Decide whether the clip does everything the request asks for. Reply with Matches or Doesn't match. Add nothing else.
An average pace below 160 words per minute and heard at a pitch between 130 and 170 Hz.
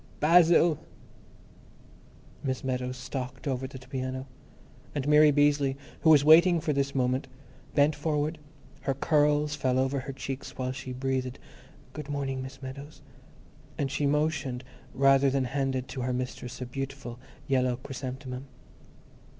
Matches